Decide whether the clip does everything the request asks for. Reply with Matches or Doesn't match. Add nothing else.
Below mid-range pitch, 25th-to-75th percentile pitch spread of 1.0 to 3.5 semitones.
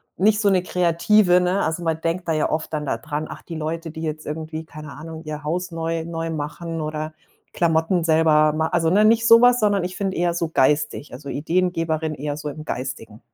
Doesn't match